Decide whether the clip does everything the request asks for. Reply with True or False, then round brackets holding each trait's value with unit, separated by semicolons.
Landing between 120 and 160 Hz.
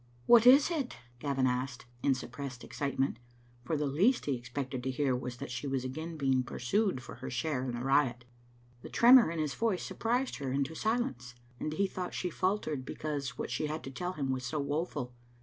True (140 Hz)